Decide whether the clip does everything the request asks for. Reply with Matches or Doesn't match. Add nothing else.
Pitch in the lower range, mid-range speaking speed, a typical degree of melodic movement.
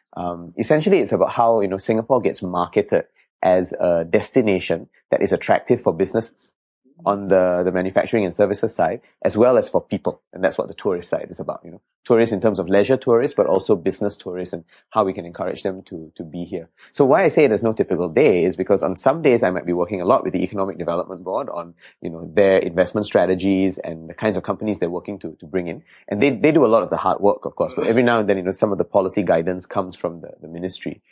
Doesn't match